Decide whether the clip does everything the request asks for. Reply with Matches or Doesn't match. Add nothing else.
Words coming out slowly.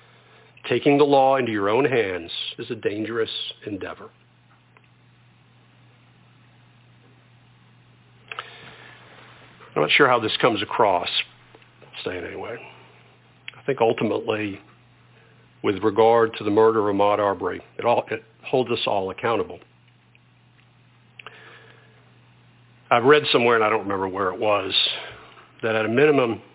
Matches